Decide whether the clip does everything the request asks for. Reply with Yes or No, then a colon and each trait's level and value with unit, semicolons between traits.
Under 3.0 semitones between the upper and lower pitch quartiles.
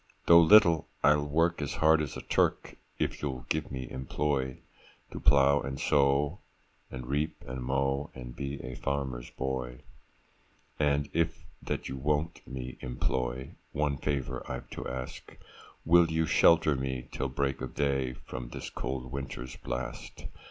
Yes: narrow, 2.4 semitones